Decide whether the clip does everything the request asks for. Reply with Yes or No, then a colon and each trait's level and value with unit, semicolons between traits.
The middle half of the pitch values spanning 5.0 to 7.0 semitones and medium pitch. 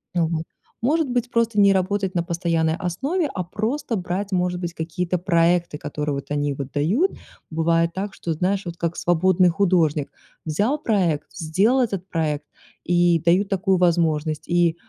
No: average, 3.4 semitones; medium, 175 Hz